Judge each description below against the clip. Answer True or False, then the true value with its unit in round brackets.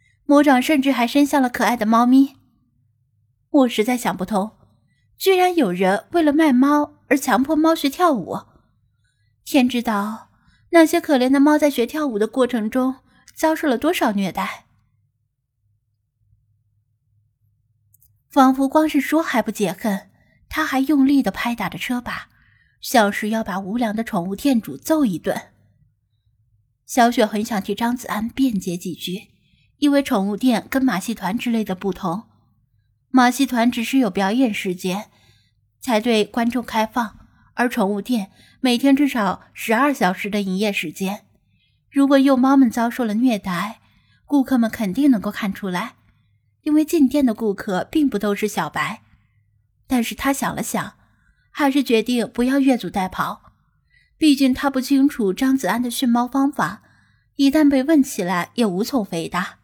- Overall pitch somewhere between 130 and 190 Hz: False (230 Hz)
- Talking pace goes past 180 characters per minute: True (225 characters per minute)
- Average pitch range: False (6.5 semitones)